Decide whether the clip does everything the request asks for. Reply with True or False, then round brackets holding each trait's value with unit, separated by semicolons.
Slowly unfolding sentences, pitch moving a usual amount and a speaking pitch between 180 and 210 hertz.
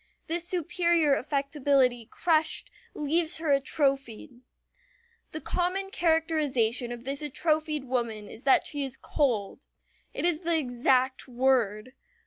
False (115 wpm; 4.2 semitones; 280 Hz)